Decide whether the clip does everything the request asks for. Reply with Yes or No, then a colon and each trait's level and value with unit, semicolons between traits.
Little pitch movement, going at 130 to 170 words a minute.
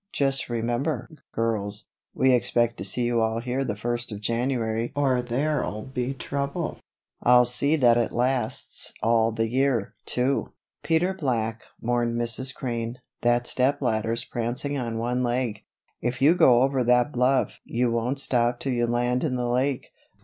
Yes: narrow, 2.1 semitones; average, 160 wpm